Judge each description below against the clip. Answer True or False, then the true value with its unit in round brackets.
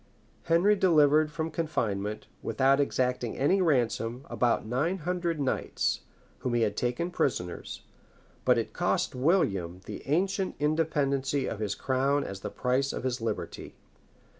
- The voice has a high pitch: False (135 Hz)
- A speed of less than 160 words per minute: True (140 wpm)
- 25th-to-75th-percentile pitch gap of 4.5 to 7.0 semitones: True (5.2 semitones)